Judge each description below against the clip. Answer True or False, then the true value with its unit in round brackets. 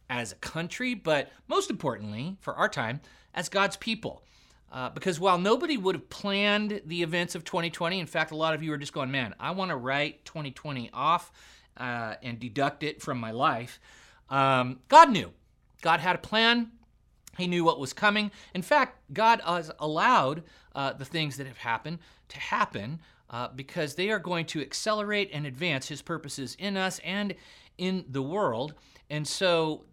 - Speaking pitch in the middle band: True (165 Hz)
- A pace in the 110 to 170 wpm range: False (180 wpm)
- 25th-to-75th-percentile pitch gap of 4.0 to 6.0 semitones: True (5.4 semitones)